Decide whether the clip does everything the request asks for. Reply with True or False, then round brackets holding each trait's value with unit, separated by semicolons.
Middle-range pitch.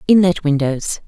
True (160 Hz)